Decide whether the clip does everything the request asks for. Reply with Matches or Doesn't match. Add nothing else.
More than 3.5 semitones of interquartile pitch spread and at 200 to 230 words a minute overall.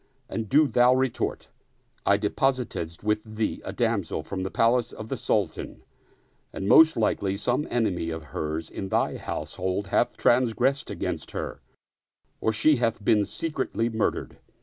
Doesn't match